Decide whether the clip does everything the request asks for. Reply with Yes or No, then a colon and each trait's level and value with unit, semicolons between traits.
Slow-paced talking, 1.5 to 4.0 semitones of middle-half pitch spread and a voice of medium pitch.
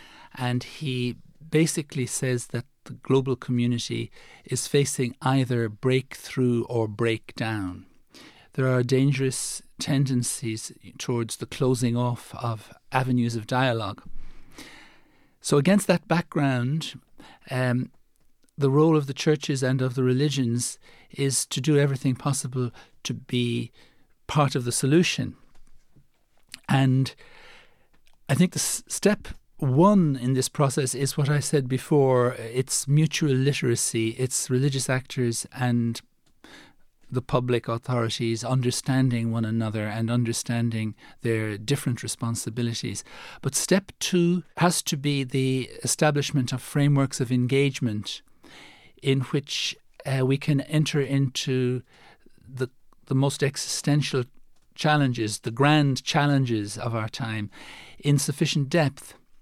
No: slow, 120 wpm; average, 3.0 semitones; low, 130 Hz